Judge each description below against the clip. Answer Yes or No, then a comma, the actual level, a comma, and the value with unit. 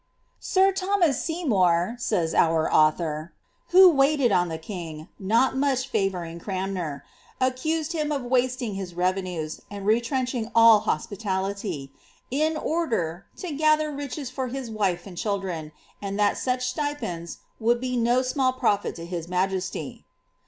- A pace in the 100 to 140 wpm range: No, average, 150 wpm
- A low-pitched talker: No, high, 220 Hz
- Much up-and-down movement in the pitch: Yes, wide, 6.9 semitones